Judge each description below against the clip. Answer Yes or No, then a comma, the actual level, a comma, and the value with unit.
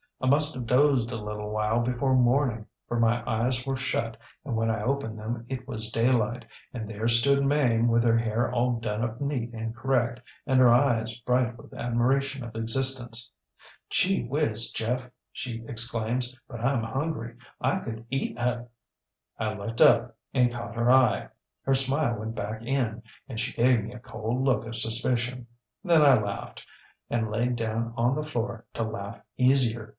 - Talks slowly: No, average, 175 wpm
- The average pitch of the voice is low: Yes, low, 120 Hz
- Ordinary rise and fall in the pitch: No, narrow, 2.3 semitones